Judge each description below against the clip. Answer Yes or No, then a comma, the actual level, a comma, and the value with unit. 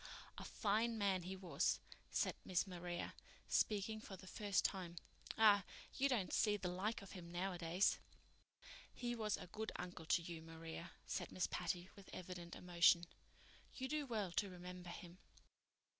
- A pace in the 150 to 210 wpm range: Yes, average, 160 wpm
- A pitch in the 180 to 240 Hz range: Yes, medium, 185 Hz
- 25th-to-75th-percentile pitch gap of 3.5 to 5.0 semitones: No, average, 3.1 semitones